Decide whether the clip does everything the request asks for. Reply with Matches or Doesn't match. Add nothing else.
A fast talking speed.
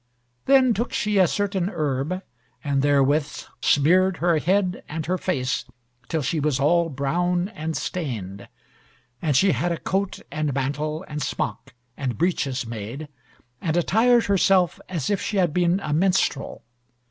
Doesn't match